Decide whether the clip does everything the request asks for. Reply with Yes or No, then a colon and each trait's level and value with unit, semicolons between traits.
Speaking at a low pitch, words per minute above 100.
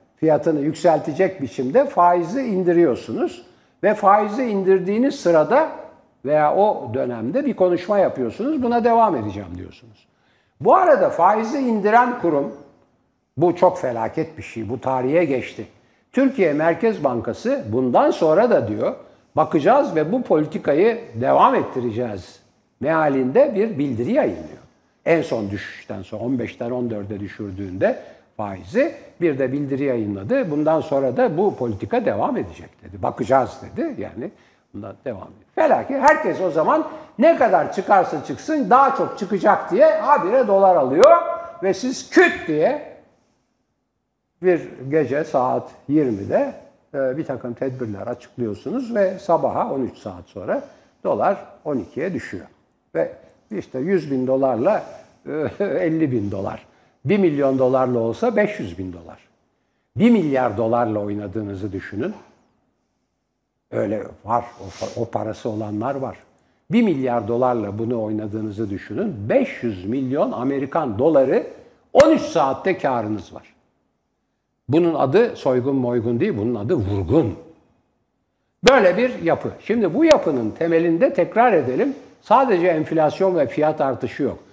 No: medium, 155 Hz; average, 125 wpm